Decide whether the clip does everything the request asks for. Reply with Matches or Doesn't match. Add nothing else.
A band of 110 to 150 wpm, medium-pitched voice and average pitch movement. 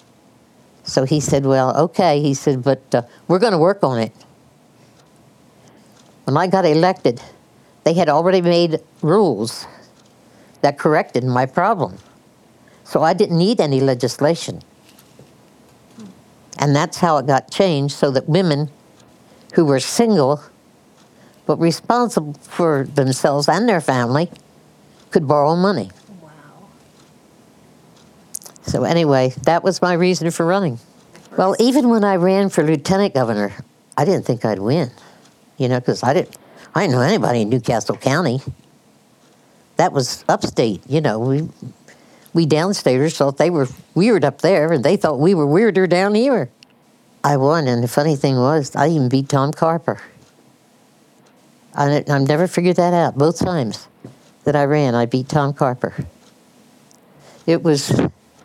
Matches